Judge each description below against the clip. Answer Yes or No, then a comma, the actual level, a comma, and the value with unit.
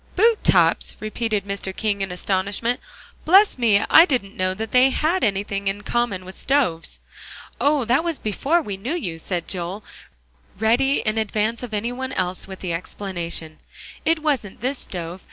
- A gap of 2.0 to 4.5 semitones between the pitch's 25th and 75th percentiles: No, wide, 5.4 semitones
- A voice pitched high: Yes, high, 215 Hz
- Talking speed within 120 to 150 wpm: No, average, 170 wpm